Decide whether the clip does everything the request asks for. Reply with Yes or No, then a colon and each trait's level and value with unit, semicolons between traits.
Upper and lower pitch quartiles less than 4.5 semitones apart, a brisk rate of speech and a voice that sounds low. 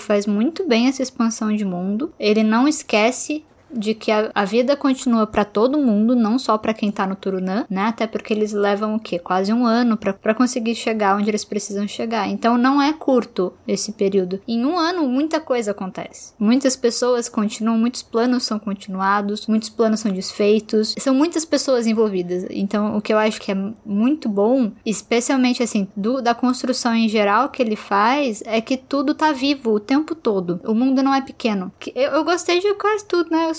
No: average, 3.9 semitones; fast, 195 wpm; high, 225 Hz